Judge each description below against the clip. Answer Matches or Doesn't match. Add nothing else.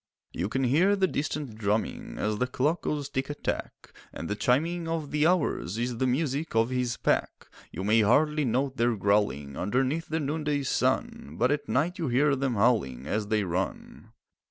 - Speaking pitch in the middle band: Doesn't match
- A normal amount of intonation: Doesn't match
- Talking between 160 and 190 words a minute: Matches